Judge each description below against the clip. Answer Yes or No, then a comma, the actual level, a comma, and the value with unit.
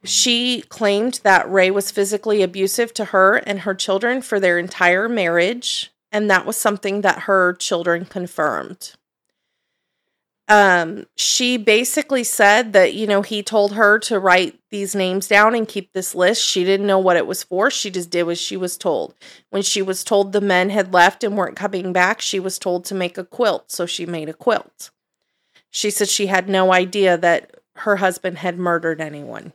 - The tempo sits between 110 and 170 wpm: No, average, 190 wpm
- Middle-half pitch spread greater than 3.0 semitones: No, narrow, 2.5 semitones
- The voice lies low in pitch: No, high, 195 Hz